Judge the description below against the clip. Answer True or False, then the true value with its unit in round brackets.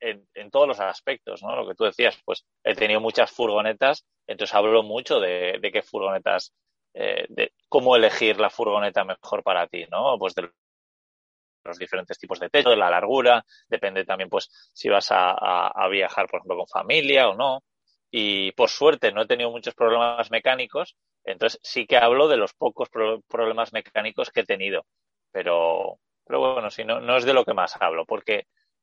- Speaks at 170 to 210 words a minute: True (190 wpm)